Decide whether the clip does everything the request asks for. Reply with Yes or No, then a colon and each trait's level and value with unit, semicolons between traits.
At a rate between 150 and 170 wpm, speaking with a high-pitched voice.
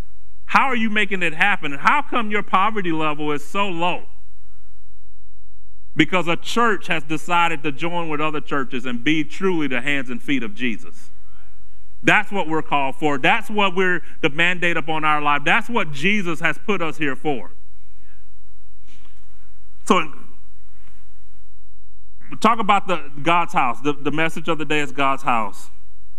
No: average, 160 wpm; medium, 145 Hz